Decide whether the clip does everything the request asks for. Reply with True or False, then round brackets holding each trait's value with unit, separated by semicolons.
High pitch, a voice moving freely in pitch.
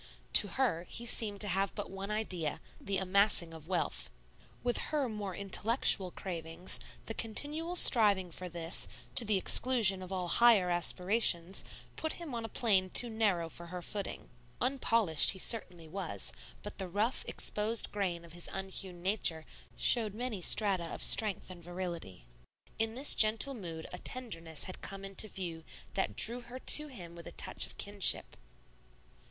False (195 Hz; 4.2 semitones)